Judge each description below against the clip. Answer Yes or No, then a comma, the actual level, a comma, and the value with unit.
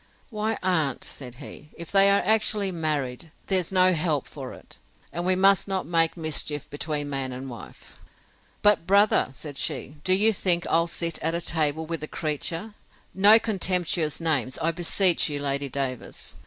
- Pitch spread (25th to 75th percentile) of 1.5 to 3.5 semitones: No, average, 4.4 semitones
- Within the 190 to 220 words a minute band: No, average, 170 wpm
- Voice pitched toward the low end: No, medium, 165 Hz